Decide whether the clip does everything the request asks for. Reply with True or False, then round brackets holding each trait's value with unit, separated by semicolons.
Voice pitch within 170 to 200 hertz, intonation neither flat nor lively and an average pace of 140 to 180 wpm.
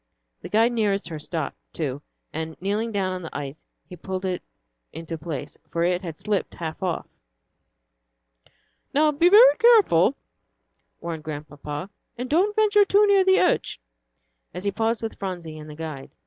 False (185 Hz; 7.1 semitones; 160 wpm)